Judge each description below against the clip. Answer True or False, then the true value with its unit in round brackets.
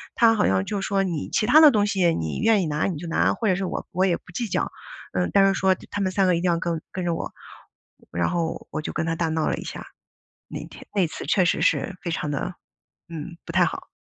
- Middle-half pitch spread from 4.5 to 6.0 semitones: False (3.0 semitones)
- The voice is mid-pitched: True (180 Hz)